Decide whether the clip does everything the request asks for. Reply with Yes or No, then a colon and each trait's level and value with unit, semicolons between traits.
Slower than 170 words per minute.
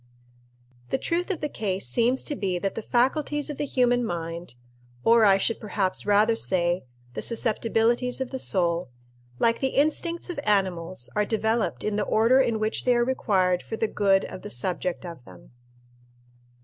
No: average, 175 wpm